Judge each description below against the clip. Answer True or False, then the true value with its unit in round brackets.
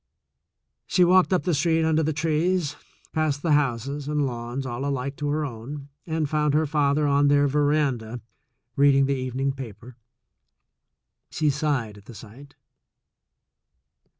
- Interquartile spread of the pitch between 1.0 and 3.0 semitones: True (2.5 semitones)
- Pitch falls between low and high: True (145 Hz)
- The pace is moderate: True (145 wpm)